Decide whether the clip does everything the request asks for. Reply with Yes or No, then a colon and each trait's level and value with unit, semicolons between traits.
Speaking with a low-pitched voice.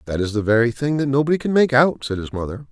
Yes: low, 130 Hz